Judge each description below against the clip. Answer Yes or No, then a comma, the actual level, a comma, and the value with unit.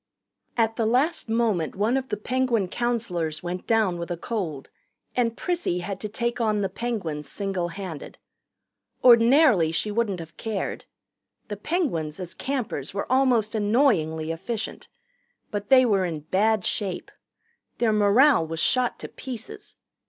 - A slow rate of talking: No, average, 145 wpm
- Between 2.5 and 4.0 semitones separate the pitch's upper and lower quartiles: No, average, 5.3 semitones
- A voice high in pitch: Yes, high, 210 Hz